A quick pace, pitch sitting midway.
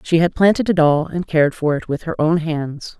Yes: fast, 260 wpm; medium, 160 Hz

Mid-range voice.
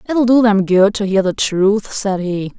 No: high, 205 Hz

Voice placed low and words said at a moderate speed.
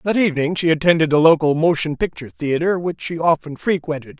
No: medium, 160 Hz; average, 185 wpm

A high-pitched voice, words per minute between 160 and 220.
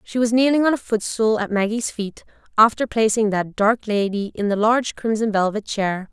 Yes: high, 215 Hz; average, 195 wpm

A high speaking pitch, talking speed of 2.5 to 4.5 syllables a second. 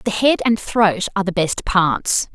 Yes: high, 195 Hz; 4.3 syllables/s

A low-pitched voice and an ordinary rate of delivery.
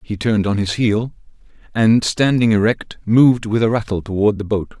Yes: low, 110 Hz; average, 190 wpm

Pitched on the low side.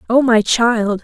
No: high, 230 Hz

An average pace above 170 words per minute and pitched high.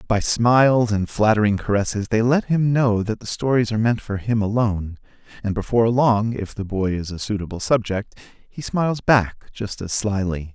No: average, 190 wpm; low, 110 Hz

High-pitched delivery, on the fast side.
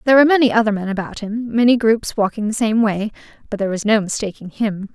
Yes: high, 220 Hz; fast, 230 wpm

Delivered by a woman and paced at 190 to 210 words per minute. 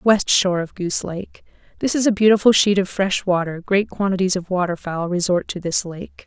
Yes: female; average, 200 wpm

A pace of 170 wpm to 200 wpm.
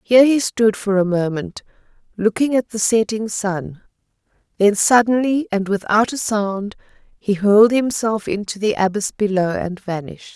No: average, 150 wpm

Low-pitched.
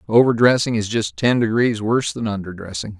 Yes: low, 115 Hz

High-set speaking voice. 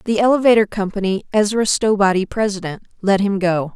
Yes: high, 200 Hz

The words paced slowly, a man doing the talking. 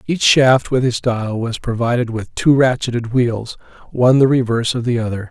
No: average, 190 wpm; male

